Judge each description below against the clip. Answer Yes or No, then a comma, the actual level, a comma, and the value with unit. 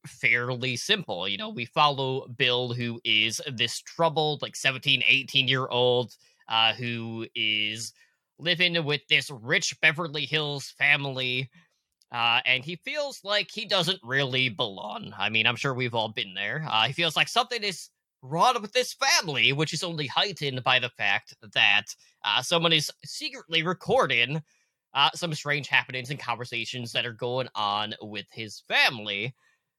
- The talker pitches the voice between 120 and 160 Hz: Yes, low, 135 Hz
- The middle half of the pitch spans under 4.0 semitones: No, average, 4.9 semitones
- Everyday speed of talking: Yes, average, 160 wpm